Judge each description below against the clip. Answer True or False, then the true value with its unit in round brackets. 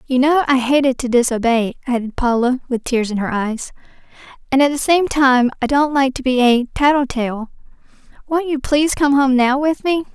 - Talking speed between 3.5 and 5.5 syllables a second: True (5.1 syllables/s)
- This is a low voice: False (265 Hz)